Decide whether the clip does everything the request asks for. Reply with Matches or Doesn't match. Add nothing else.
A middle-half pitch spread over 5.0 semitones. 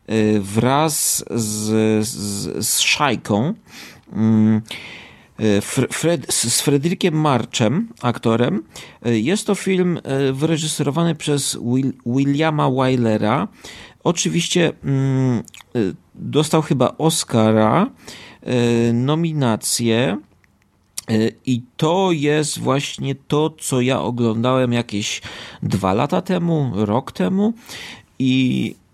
Matches